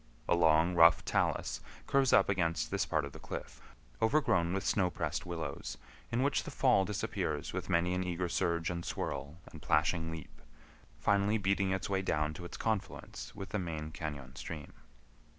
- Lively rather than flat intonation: No, average, 3.4 semitones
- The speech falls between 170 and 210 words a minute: Yes, average, 175 wpm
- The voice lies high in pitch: No, very low, 85 Hz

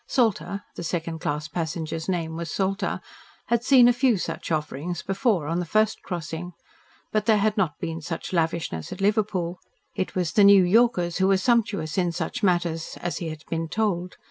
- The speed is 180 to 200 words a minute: Yes, average, 185 wpm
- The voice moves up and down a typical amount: Yes, average, 3.9 semitones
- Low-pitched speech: No, medium, 180 Hz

